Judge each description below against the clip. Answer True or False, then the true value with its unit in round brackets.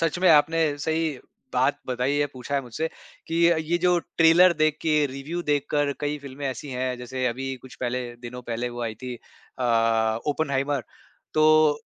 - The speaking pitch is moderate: True (145 Hz)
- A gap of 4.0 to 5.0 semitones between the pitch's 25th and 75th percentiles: False (3.5 semitones)